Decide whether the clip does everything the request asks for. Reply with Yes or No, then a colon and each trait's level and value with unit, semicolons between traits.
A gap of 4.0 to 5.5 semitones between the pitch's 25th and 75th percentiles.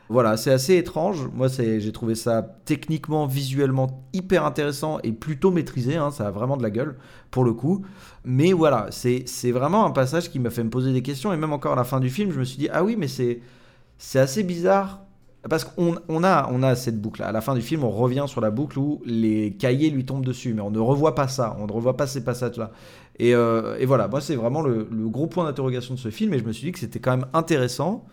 Yes: average, 4.7 semitones